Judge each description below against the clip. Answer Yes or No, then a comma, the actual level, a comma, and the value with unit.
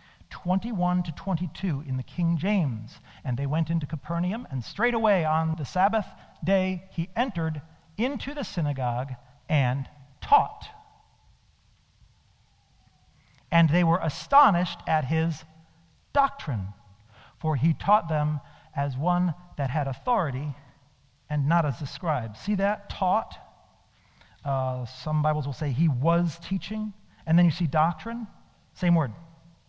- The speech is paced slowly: Yes, slow, 130 wpm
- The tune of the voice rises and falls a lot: No, average, 4.6 semitones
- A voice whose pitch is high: No, medium, 160 Hz